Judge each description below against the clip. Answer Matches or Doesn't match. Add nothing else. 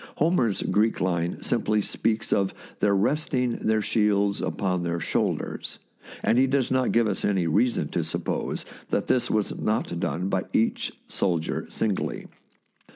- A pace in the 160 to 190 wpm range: Doesn't match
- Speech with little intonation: Doesn't match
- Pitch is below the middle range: Matches